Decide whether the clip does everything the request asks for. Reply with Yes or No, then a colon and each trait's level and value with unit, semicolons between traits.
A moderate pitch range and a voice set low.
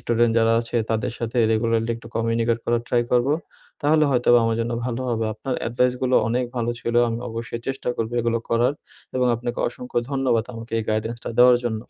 No: narrow, 1.5 semitones; low, 120 Hz